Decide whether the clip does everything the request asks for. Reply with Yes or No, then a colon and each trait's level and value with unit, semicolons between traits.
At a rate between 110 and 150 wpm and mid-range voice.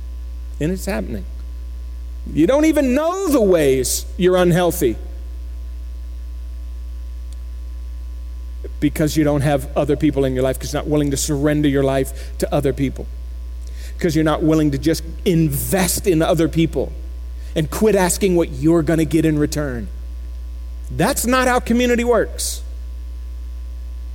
No: slow, 135 wpm; low, 120 Hz